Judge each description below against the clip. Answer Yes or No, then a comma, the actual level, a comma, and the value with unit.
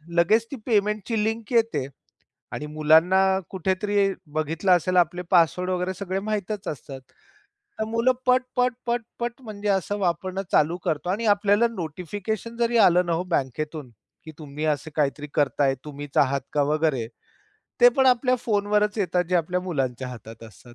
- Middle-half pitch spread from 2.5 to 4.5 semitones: No, wide, 5.6 semitones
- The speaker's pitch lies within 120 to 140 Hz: No, medium, 180 Hz